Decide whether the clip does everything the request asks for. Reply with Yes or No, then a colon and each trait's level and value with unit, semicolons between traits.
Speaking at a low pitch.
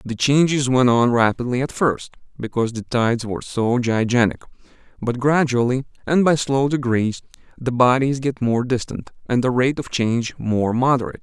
Yes: low, 125 Hz